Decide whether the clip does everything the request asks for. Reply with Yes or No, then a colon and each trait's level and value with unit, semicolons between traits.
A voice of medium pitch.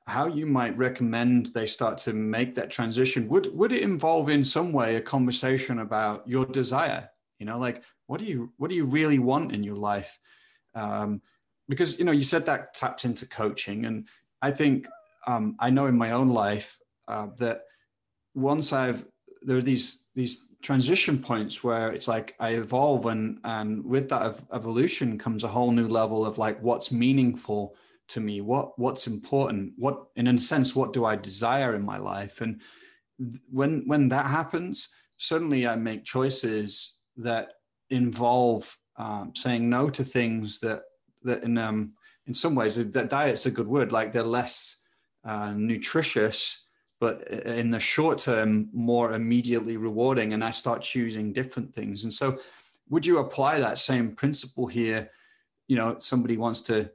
No: low, 120 Hz